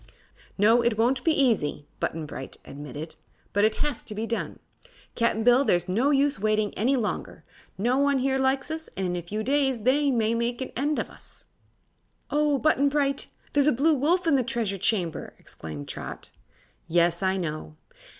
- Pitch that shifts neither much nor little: No, wide, 6.2 semitones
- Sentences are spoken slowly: No, average, 185 wpm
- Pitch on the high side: Yes, high, 235 Hz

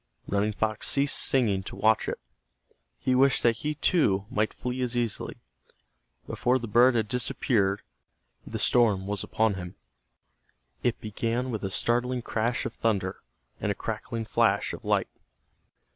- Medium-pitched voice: No, low, 115 Hz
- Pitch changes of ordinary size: Yes, average, 3.2 semitones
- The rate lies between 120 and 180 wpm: Yes, average, 150 wpm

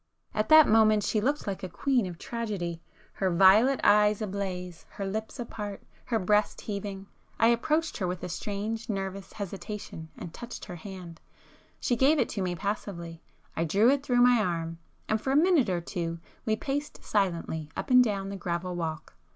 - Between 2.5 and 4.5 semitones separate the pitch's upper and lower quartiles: Yes, average, 4.1 semitones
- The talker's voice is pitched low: No, high, 200 Hz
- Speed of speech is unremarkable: Yes, average, 165 wpm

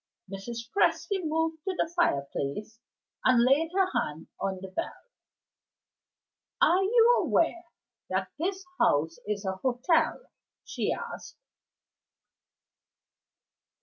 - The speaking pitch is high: Yes, very high, 305 Hz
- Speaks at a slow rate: Yes, slow, 105 wpm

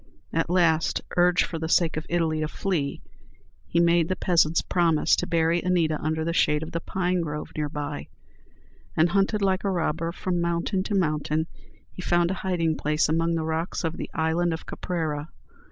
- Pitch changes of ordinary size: No, narrow, 1.9 semitones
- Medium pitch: Yes, medium, 165 Hz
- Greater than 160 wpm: Yes, average, 185 wpm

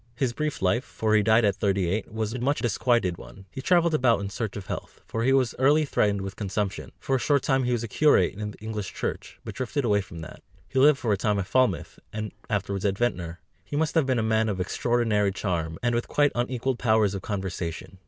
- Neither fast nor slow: No, fast, 240 wpm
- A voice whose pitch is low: Yes, low, 110 Hz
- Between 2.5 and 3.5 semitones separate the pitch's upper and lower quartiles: No, average, 4.5 semitones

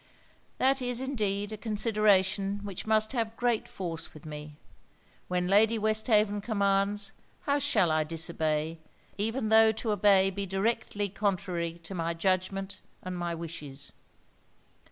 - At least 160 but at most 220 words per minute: No, slow, 135 wpm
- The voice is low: No, high, 200 Hz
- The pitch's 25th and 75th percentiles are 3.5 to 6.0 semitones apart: Yes, average, 3.8 semitones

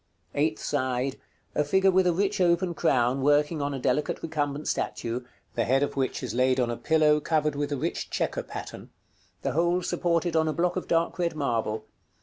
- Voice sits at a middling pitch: Yes, medium, 150 Hz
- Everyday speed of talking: Yes, average, 195 wpm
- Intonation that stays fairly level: No, average, 4.4 semitones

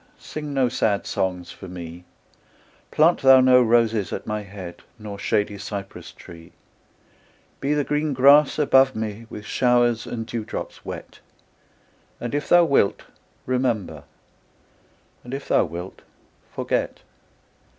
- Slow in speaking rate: Yes, slow, 130 wpm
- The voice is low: Yes, low, 115 Hz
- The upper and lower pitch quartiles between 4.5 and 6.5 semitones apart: Yes, average, 5.0 semitones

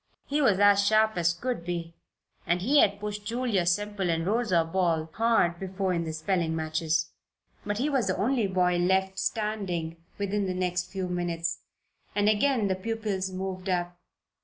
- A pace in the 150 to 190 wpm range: Yes, average, 170 wpm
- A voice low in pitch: No, high, 190 Hz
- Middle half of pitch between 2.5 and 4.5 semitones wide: Yes, average, 3.1 semitones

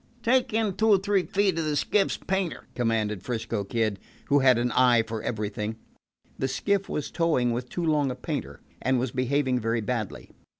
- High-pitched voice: No, low, 130 Hz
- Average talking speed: Yes, average, 185 wpm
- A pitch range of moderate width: No, wide, 6.8 semitones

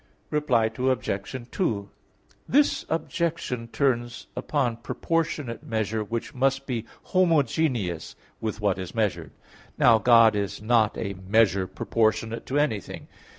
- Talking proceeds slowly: Yes, slow, 115 wpm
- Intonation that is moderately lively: Yes, average, 4.4 semitones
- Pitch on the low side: Yes, low, 115 Hz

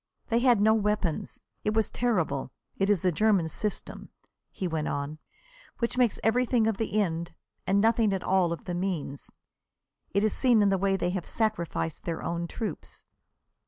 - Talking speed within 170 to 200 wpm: Yes, average, 175 wpm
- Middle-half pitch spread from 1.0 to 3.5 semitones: No, average, 4.4 semitones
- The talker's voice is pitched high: Yes, high, 195 Hz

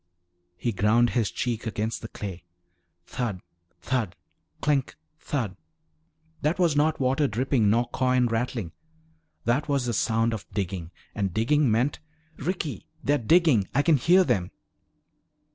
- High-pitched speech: No, low, 120 Hz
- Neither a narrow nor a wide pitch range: Yes, average, 4.7 semitones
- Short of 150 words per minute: Yes, slow, 135 wpm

